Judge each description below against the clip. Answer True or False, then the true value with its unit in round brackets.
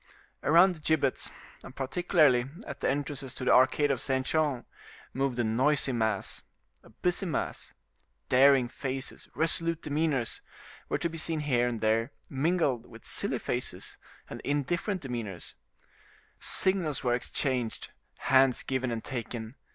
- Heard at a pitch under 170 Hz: True (135 Hz)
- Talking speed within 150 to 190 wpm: False (140 wpm)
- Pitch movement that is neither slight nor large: True (4.2 semitones)